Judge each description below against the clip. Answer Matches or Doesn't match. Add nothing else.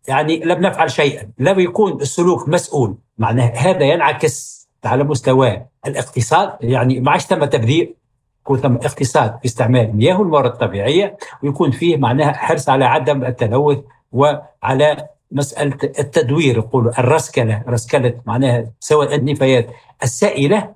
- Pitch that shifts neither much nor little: Matches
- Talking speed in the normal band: Matches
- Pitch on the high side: Doesn't match